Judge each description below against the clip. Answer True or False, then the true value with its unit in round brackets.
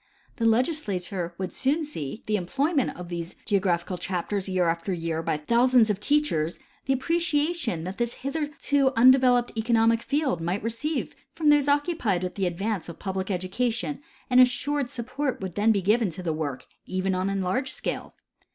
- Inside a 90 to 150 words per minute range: False (170 wpm)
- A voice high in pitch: True (220 Hz)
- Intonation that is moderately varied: False (6.6 semitones)